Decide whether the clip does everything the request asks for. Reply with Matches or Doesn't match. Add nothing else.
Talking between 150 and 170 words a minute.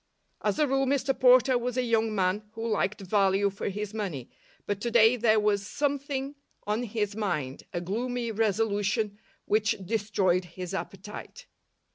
Matches